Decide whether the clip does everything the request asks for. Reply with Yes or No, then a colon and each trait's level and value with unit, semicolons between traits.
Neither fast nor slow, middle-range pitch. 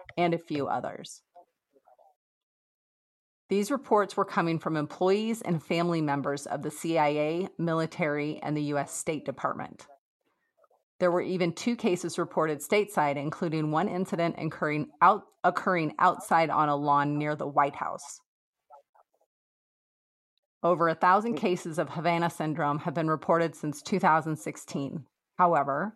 No: slow, 130 wpm; medium, 165 Hz